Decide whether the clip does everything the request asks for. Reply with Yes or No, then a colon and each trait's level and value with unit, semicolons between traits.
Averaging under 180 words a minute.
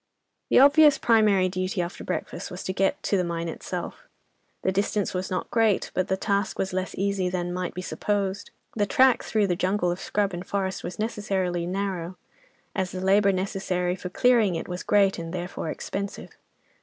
No: average, 185 wpm